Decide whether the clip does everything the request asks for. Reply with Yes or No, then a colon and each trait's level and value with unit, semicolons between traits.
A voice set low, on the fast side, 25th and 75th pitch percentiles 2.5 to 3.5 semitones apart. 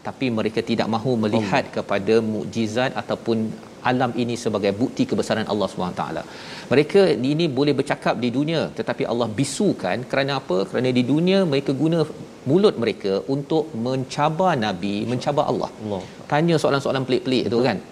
No: low, 130 Hz; fast, 145 wpm; average, 4.4 semitones